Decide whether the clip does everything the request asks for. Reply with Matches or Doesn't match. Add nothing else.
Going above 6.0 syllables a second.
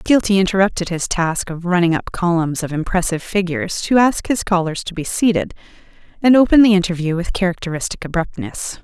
Doesn't match